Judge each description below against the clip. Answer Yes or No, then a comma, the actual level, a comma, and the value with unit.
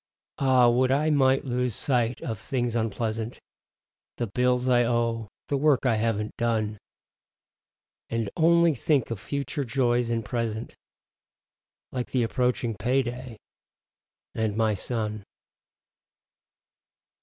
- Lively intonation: No, narrow, 2.4 semitones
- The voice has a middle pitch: No, low, 120 Hz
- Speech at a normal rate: No, slow, 115 wpm